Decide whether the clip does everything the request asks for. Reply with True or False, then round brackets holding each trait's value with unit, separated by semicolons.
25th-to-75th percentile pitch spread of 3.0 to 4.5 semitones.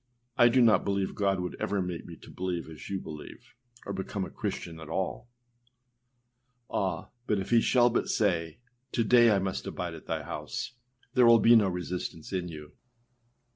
True (4.2 semitones)